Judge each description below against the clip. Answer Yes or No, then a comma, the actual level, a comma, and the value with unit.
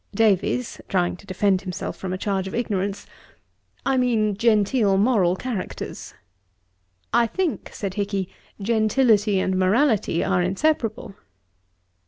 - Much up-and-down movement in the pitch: No, average, 3.5 semitones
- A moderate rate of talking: No, slow, 120 wpm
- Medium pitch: No, high, 205 Hz